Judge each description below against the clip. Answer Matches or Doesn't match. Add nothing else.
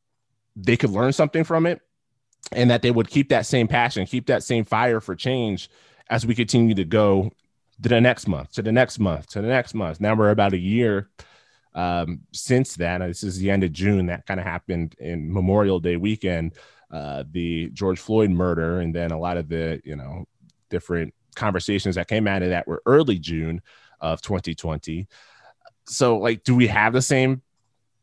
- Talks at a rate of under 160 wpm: Doesn't match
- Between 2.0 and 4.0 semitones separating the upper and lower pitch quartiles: Doesn't match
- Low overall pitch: Matches